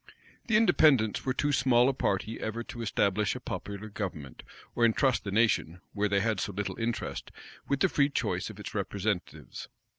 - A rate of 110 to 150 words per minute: No, average, 180 wpm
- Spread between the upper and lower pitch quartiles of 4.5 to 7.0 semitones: No, average, 4.1 semitones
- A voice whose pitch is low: Yes, low, 110 Hz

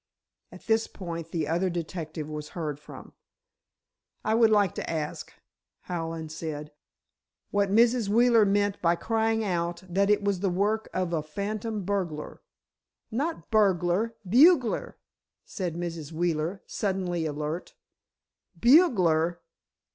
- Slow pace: Yes, slow, 120 wpm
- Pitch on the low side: No, medium, 185 Hz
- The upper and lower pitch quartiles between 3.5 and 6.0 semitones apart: Yes, average, 4.6 semitones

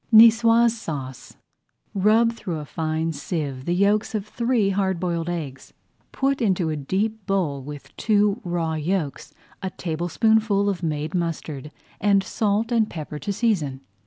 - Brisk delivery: No, average, 145 wpm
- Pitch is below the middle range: No, medium, 185 Hz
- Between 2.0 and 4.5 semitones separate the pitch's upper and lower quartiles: No, wide, 5.4 semitones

